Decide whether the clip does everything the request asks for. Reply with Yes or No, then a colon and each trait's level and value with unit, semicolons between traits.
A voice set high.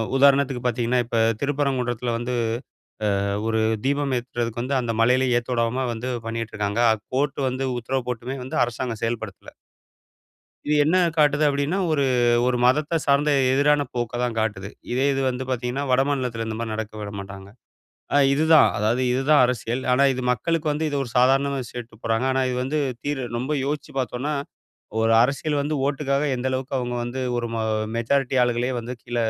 No: low, 125 Hz